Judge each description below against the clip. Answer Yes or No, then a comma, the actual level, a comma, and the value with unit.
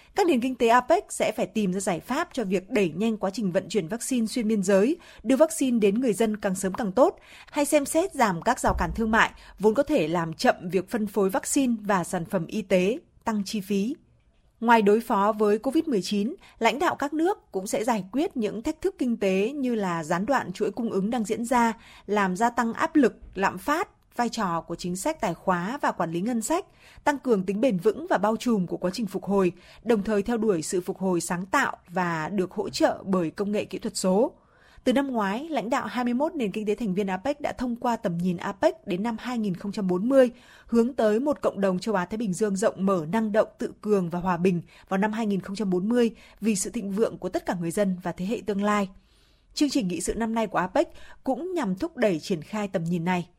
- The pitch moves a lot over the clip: No, average, 4.5 semitones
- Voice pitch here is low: No, high, 215 Hz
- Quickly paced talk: No, average, 235 wpm